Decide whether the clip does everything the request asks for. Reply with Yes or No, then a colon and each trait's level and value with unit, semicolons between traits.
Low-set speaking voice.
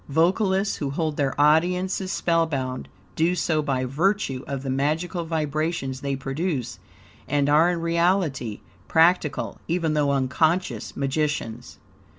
No: medium, 155 Hz